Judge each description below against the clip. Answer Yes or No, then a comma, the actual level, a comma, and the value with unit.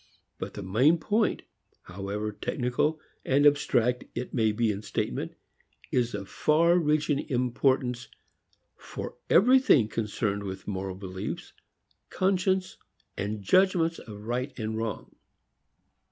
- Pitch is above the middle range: No, low, 125 Hz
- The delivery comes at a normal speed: No, slow, 115 wpm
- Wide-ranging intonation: Yes, wide, 6.6 semitones